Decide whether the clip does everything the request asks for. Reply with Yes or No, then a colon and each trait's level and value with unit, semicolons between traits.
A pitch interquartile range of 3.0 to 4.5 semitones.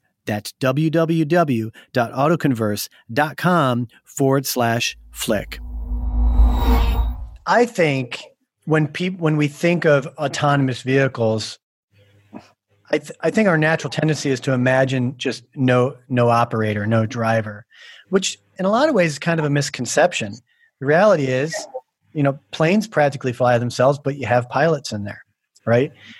No: average, 5.3 semitones